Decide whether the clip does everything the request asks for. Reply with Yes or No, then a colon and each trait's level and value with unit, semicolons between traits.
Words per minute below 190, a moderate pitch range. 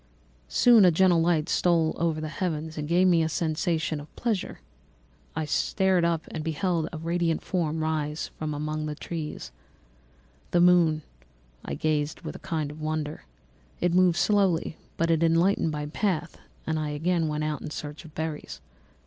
No: average, 170 wpm; narrow, 2.2 semitones